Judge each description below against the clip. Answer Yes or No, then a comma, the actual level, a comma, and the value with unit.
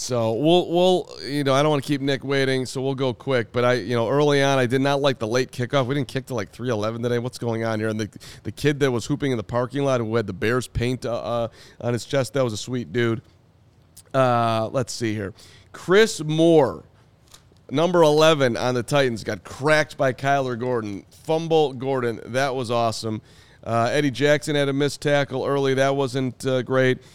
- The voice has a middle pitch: No, low, 130 Hz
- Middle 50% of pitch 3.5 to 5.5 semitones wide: No, average, 3.1 semitones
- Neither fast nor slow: No, fast, 220 wpm